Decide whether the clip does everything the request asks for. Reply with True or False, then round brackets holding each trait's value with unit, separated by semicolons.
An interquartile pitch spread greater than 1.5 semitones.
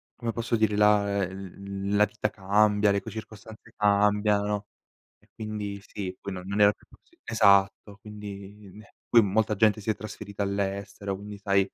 False (1.2 semitones)